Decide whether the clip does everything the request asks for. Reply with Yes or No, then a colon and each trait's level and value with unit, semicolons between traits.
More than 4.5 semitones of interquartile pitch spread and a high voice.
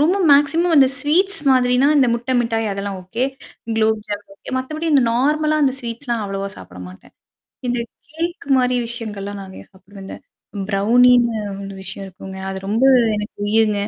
Yes: average, 5.3 semitones; high, 235 Hz